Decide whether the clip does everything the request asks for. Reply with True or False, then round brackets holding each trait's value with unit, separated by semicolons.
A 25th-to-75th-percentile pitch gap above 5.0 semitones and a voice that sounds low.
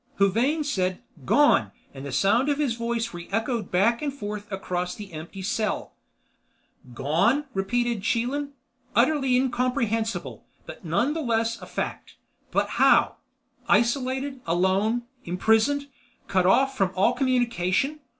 False (5.4 semitones; 230 Hz)